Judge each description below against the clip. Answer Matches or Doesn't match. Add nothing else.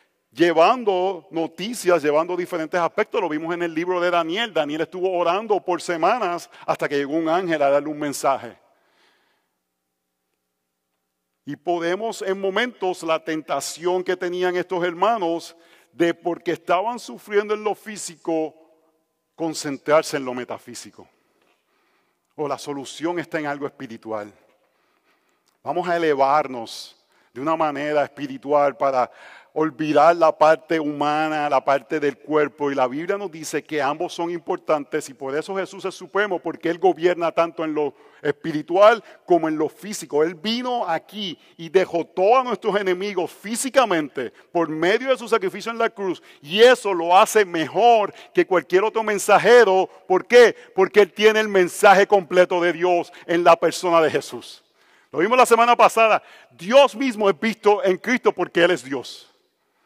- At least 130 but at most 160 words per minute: Matches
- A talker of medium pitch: Matches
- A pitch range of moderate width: Matches